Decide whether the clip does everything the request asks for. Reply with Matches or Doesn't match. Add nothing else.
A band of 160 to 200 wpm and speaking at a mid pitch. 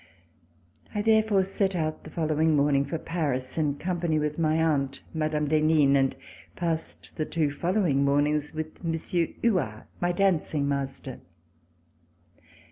Doesn't match